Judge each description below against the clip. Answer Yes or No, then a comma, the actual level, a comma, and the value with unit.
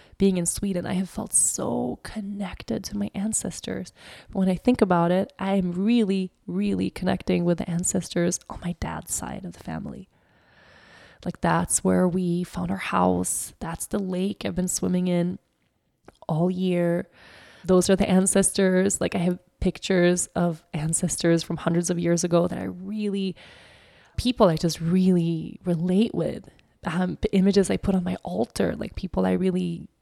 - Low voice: No, medium, 180 Hz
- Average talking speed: Yes, average, 165 wpm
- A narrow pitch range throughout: Yes, narrow, 2.0 semitones